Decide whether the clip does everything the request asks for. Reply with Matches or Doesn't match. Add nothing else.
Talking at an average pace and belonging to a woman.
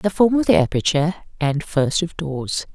Matches